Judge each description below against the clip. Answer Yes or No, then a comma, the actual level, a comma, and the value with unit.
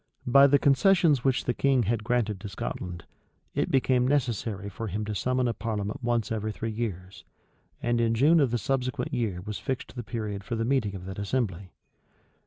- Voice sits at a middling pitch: No, low, 115 Hz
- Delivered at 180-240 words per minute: Yes, average, 190 wpm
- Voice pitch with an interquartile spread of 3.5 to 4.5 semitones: Yes, average, 3.8 semitones